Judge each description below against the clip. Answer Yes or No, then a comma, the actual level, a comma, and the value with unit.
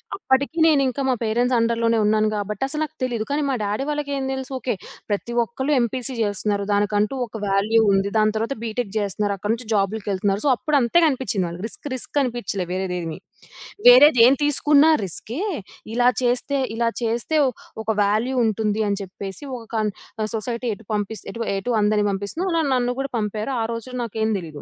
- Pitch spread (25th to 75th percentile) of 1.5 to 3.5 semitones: No, average, 4.0 semitones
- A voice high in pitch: Yes, high, 230 Hz